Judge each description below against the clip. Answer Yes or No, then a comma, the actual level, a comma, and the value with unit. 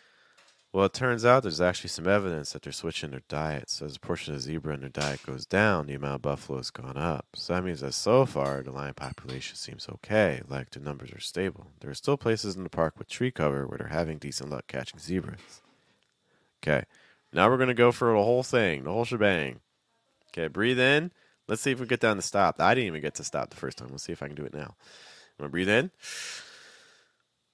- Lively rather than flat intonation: Yes, wide, 8.0 semitones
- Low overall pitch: Yes, very low, 85 Hz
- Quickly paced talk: Yes, fast, 240 wpm